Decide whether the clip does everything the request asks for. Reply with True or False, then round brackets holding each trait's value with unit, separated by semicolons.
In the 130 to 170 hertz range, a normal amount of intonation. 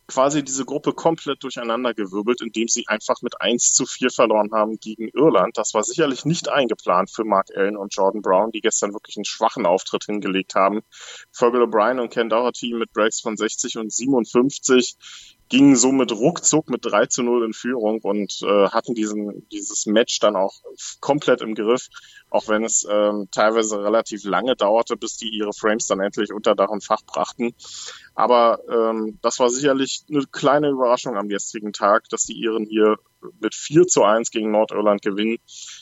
False (115 Hz; 3.3 semitones)